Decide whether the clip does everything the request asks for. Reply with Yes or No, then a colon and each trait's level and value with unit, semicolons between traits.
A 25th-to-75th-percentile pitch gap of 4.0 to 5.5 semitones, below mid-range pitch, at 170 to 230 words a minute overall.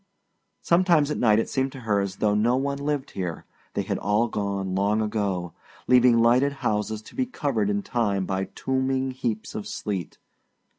Yes: average, 4.6 semitones; low, 110 Hz; average, 185 wpm